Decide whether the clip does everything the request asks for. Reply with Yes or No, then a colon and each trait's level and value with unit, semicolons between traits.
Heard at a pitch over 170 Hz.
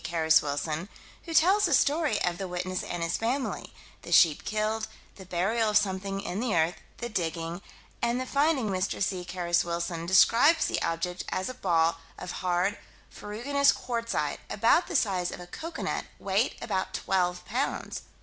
Yes: high, 190 Hz